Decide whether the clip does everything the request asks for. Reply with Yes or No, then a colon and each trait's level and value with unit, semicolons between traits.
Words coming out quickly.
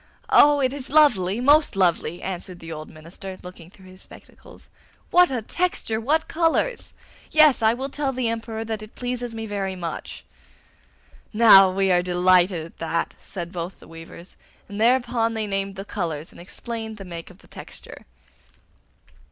No: average, 170 wpm